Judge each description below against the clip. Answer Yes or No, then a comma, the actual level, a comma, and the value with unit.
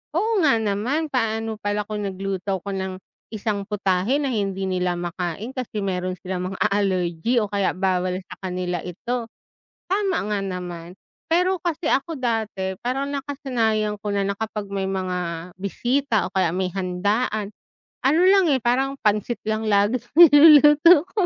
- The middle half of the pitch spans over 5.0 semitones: Yes, wide, 5.4 semitones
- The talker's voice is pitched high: Yes, high, 210 Hz